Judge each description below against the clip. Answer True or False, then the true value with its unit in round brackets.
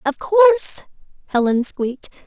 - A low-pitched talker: False (315 Hz)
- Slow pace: True (105 wpm)